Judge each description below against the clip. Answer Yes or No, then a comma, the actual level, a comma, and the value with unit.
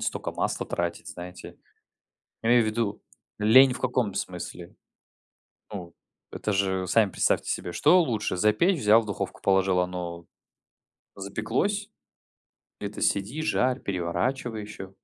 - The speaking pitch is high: No, low, 105 Hz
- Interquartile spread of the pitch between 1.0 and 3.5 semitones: No, average, 4.3 semitones